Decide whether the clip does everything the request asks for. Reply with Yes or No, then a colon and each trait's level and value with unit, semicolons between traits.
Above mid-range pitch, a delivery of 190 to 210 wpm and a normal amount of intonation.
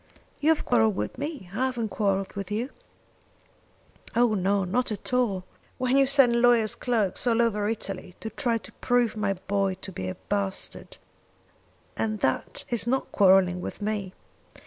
No: high, 215 Hz; average, 165 wpm; average, 3.8 semitones